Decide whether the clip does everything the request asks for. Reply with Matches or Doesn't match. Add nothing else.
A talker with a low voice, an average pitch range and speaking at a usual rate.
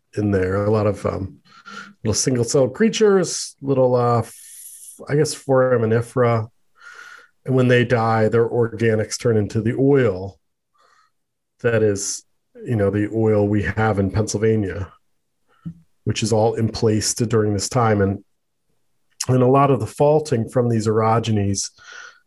Matches